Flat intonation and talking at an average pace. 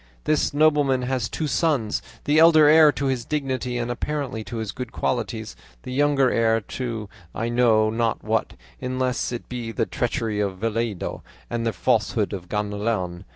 No: average, 3.5 semitones; average, 165 wpm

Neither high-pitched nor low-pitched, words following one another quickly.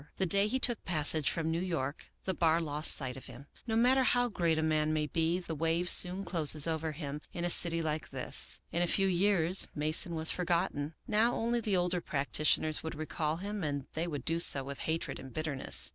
Yes: medium, 165 Hz; fast, 215 wpm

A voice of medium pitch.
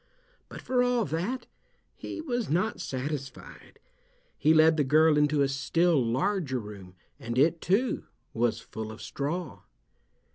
Yes: medium, 150 Hz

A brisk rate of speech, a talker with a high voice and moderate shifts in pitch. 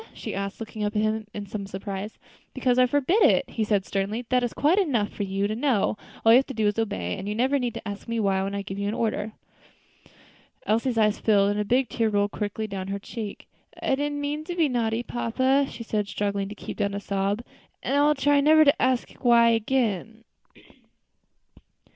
Yes: fast, 225 wpm; high, 220 Hz; average, 4.0 semitones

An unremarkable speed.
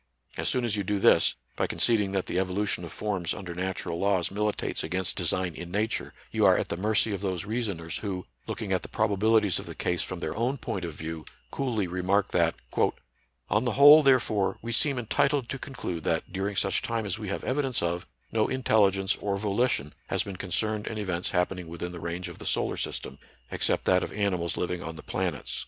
No: fast, 215 wpm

